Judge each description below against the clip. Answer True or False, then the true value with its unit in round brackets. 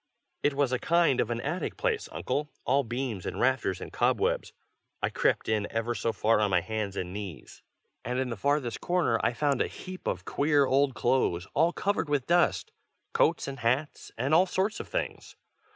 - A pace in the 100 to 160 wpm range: False (195 wpm)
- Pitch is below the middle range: True (130 Hz)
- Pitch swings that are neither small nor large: True (4.8 semitones)